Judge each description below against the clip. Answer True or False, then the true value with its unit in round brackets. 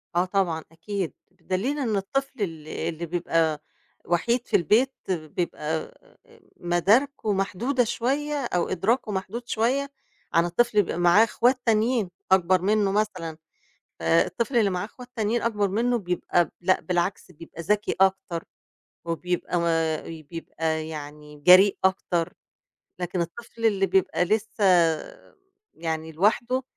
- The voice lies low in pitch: False (190 Hz)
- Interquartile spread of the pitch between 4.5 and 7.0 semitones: True (5.0 semitones)